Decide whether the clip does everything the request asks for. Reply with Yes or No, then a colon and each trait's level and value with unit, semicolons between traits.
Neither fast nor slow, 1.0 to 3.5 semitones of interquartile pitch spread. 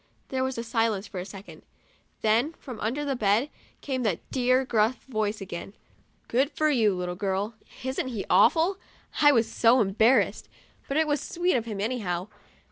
No: average, 175 wpm; average, 4.4 semitones